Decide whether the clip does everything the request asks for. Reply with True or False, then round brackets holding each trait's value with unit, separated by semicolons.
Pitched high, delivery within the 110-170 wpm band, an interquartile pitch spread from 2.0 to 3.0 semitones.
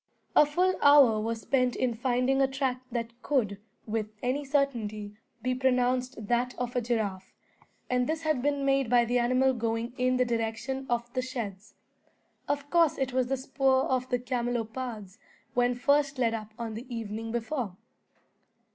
True (250 Hz; 165 wpm; 2.7 semitones)